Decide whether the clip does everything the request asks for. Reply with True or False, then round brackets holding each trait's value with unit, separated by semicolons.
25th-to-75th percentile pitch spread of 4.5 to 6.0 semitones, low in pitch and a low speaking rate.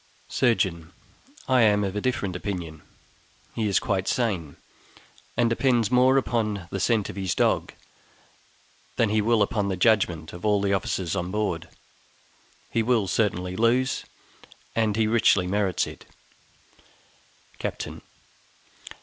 False (3.8 semitones; 105 Hz; 130 wpm)